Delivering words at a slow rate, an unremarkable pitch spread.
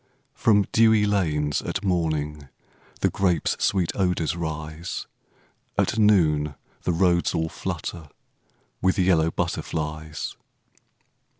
Yes: slow, 100 wpm; average, 3.4 semitones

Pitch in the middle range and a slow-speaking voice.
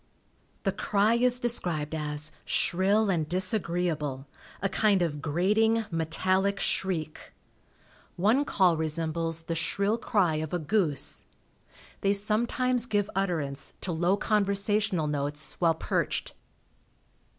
Yes: medium, 180 Hz; slow, 115 wpm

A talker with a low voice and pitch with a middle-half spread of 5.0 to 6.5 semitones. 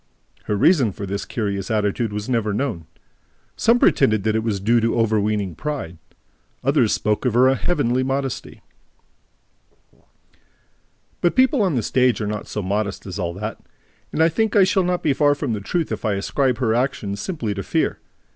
Yes: low, 115 Hz; wide, 5.4 semitones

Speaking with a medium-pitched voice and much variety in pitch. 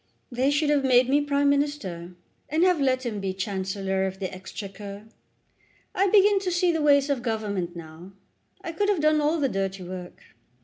No: very high, 250 Hz; wide, 7.6 semitones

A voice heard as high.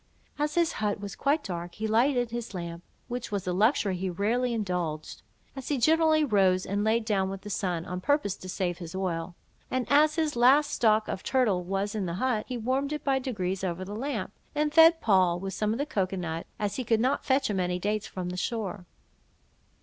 Yes: high, 210 Hz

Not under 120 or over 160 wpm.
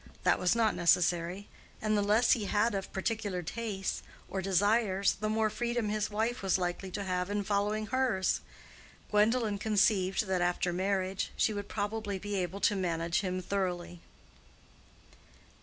Yes: average, 155 wpm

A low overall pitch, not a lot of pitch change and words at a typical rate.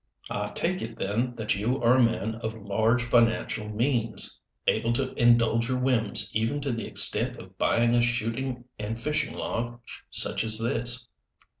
Yes: low, 115 Hz; narrow, 1.6 semitones; average, 165 wpm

